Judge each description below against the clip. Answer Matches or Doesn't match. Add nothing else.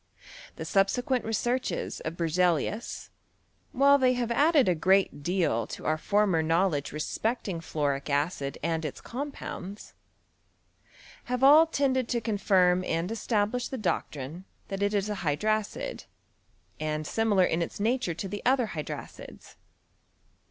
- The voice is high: Matches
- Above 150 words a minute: Doesn't match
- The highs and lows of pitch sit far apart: Matches